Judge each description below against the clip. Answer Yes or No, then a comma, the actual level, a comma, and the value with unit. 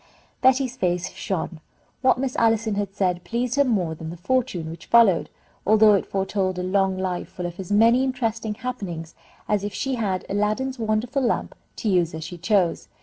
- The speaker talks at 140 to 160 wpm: No, average, 185 wpm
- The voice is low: No, high, 205 Hz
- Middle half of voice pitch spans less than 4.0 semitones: No, average, 4.5 semitones